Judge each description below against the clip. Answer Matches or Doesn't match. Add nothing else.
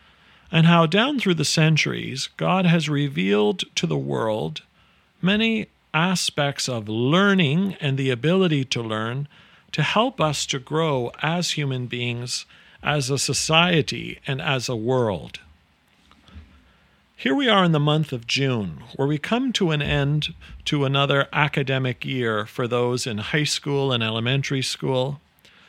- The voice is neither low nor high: Matches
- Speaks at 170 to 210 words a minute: Doesn't match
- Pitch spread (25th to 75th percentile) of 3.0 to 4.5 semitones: Doesn't match